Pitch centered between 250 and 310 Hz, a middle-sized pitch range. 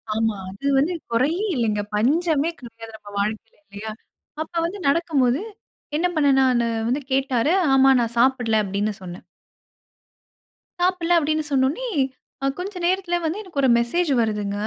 No: very high, 265 Hz; wide, 6.8 semitones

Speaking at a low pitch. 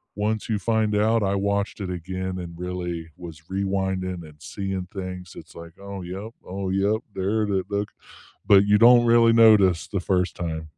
Yes: very low, 95 Hz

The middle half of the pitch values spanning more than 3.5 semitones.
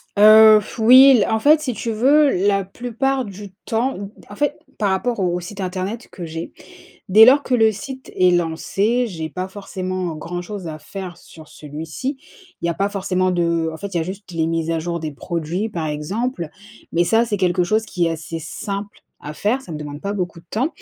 Yes: average, 4.7 semitones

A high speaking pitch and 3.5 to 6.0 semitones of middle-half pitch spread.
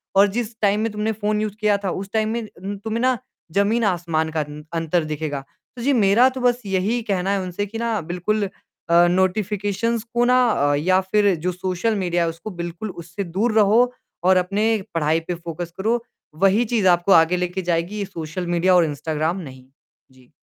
Yes: high, 195 Hz; average, 3.9 semitones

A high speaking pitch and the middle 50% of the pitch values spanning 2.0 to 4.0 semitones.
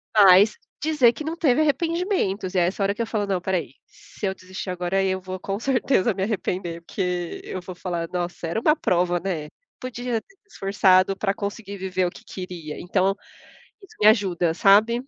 Yes: high, 195 Hz; average, 3.7 semitones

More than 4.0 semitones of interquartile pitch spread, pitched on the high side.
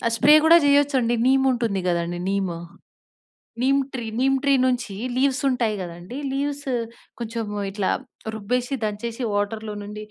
Yes: average, 4.8 semitones; high, 235 Hz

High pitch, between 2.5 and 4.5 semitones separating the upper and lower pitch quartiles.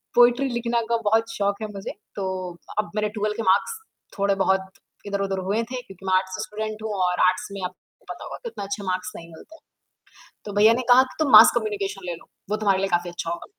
Yes: high, 200 Hz; average, 2.8 semitones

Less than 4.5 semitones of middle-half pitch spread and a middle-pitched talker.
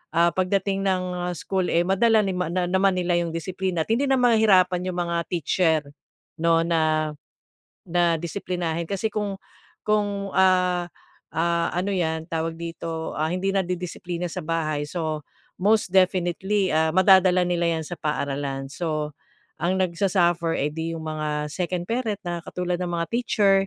Yes: narrow, 2.5 semitones; medium, 175 Hz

